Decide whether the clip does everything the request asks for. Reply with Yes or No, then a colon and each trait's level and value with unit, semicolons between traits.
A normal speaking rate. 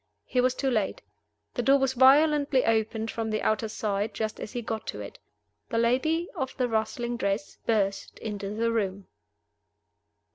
Yes: average, 170 wpm